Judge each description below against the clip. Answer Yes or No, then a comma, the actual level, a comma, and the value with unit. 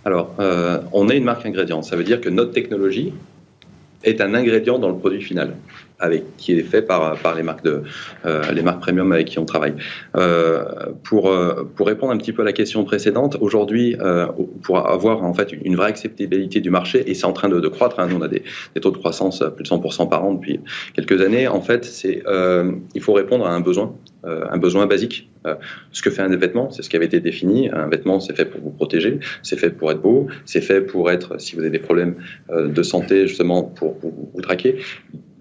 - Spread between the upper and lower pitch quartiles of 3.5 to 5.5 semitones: No, narrow, 2.6 semitones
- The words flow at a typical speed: No, fast, 235 wpm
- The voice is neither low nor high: No, very low, 90 Hz